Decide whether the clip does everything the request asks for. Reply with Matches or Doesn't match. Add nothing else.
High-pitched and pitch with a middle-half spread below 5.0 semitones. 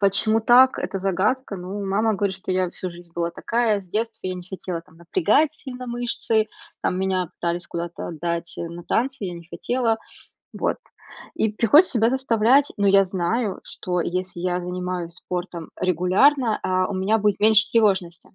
Matches